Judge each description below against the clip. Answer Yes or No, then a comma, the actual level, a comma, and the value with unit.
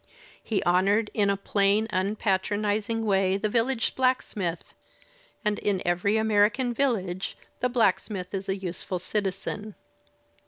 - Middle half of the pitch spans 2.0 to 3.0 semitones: Yes, narrow, 2.5 semitones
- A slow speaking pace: Yes, slow, 120 wpm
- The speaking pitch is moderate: No, high, 205 Hz